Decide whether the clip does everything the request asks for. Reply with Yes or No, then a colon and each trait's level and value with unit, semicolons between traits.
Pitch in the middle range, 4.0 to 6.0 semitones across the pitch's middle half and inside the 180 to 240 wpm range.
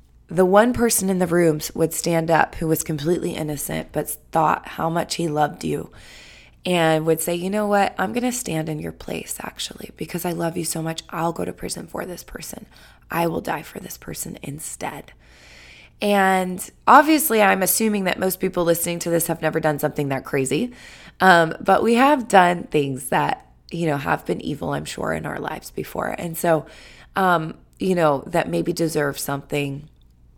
No: medium, 170 Hz; average, 3.3 semitones; average, 190 wpm